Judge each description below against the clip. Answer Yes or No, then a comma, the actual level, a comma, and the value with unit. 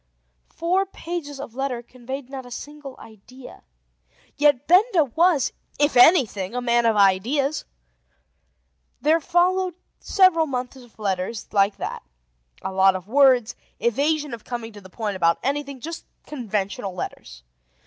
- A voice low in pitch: No, very high, 255 Hz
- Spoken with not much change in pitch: No, wide, 5.6 semitones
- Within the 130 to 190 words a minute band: Yes, average, 140 wpm